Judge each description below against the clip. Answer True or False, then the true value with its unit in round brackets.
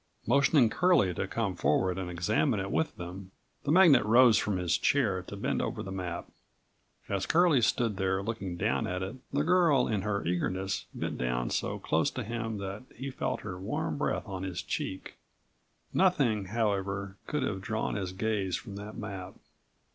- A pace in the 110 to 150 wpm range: False (175 wpm)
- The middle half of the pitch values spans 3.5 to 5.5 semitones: True (4.2 semitones)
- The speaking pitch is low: True (100 Hz)